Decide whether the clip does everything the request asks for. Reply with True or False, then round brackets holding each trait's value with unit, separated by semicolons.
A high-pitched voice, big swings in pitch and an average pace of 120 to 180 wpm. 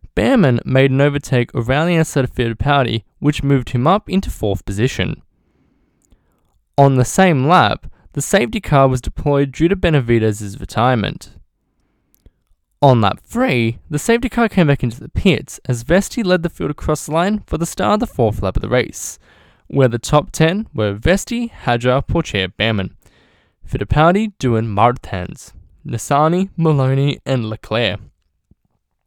False (135 Hz; 6.2 semitones; 155 wpm)